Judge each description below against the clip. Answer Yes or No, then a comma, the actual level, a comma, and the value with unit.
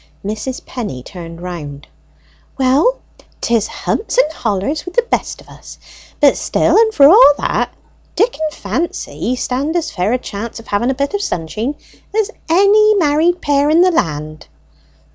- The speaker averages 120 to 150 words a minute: No, average, 160 wpm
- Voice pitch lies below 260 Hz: No, very high, 280 Hz